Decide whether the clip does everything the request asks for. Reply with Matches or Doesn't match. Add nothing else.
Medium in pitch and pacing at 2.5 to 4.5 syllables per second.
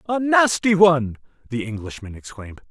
Doesn't match